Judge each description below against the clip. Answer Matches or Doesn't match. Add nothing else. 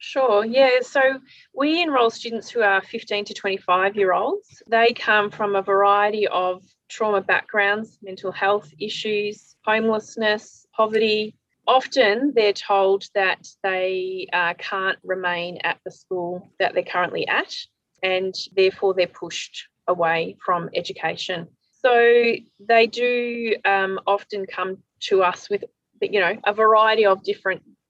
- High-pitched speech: Matches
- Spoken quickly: Doesn't match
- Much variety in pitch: Doesn't match